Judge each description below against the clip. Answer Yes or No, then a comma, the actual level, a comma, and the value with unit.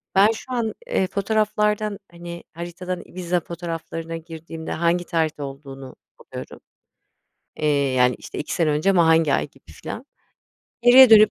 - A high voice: No, medium, 170 Hz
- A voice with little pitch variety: No, average, 4.0 semitones